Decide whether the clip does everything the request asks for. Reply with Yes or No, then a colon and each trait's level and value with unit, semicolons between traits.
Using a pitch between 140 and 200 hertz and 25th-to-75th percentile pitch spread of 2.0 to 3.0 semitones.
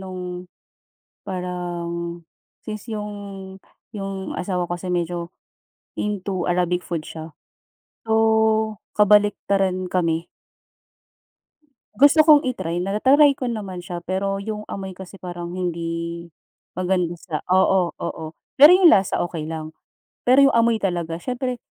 No: medium, 185 Hz; average, 3.6 semitones